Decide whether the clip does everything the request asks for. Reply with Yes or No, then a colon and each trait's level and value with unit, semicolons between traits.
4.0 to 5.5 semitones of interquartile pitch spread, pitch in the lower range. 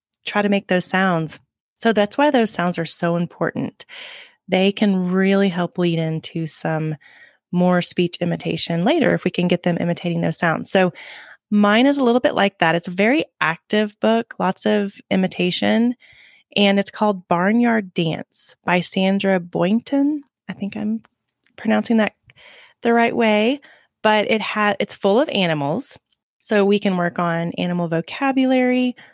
No: average, 4.6 semitones; high, 200 Hz